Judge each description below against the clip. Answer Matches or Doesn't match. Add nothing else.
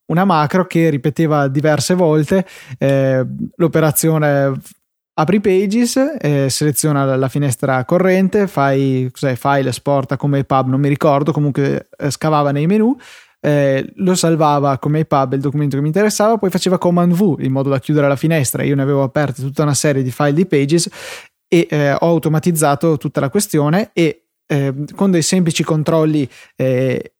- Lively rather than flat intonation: Doesn't match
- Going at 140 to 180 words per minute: Matches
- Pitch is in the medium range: Matches